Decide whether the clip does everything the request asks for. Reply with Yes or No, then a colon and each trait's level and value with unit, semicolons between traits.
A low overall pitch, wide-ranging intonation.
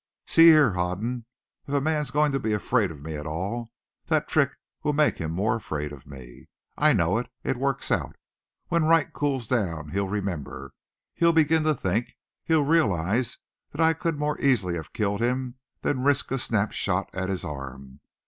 Yes: low, 110 Hz; wide, 8.6 semitones